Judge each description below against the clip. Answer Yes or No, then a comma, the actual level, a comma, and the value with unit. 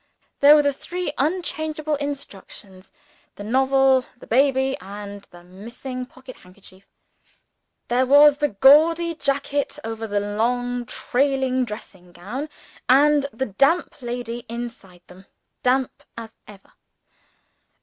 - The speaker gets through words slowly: Yes, slow, 120 wpm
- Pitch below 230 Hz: No, very high, 255 Hz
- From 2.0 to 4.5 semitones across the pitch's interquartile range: No, average, 5.3 semitones